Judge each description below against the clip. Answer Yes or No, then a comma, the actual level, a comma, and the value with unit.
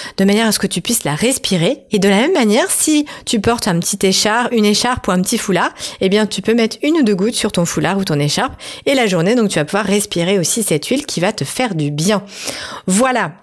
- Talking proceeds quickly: Yes, fast, 265 wpm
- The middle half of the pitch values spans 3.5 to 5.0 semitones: Yes, average, 3.8 semitones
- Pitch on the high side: Yes, high, 210 Hz